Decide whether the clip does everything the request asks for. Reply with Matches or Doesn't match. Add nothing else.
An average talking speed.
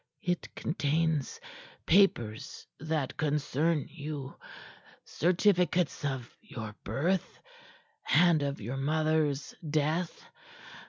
Doesn't match